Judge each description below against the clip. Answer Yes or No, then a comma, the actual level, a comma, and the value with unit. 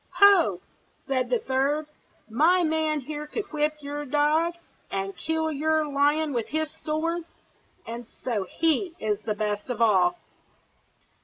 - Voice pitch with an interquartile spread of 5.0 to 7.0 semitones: No, average, 4.3 semitones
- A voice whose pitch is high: Yes, very high, 295 Hz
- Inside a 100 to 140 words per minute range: Yes, slow, 135 wpm